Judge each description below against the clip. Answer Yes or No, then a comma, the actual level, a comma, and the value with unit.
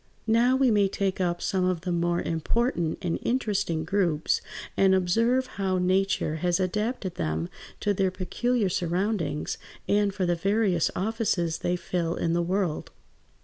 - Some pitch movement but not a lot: Yes, average, 3.1 semitones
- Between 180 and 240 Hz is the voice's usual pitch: Yes, medium, 185 Hz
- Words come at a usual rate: Yes, average, 150 wpm